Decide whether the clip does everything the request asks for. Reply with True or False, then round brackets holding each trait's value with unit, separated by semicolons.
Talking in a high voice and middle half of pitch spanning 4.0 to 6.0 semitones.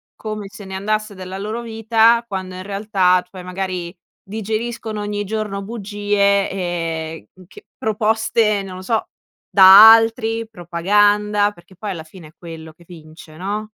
False (200 Hz; 2.8 semitones)